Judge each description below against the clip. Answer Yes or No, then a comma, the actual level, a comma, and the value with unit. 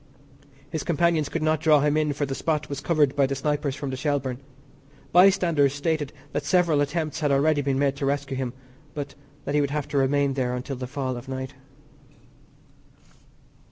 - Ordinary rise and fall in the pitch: No, narrow, 2.0 semitones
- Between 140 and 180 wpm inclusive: No, average, 190 wpm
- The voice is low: No, medium, 145 Hz